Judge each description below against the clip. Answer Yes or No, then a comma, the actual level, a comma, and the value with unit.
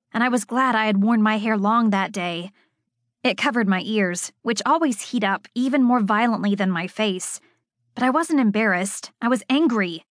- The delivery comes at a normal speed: Yes, average, 195 wpm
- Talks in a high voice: Yes, high, 220 Hz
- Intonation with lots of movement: No, average, 4.3 semitones